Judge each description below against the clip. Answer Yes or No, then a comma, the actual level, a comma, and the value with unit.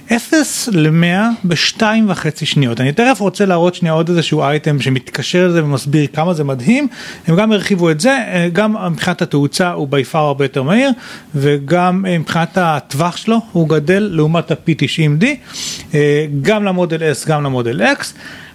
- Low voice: No, medium, 170 Hz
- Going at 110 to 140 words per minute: No, fast, 150 wpm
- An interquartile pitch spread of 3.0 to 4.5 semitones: No, average, 5.2 semitones